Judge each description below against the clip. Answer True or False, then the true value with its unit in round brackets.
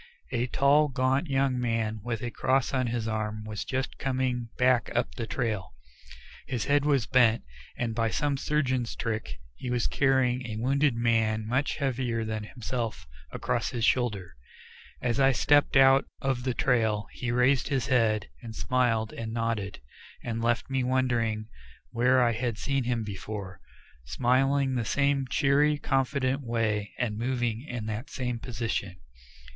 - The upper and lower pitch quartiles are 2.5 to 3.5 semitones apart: True (2.9 semitones)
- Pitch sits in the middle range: False (120 Hz)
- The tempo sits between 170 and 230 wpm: False (160 wpm)